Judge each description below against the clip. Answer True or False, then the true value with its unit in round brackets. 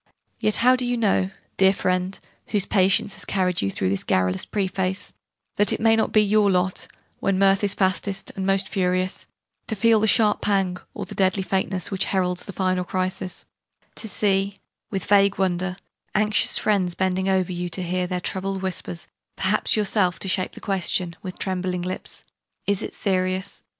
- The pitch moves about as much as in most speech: False (1.6 semitones)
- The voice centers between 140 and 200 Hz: True (190 Hz)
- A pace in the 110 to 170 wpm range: False (180 wpm)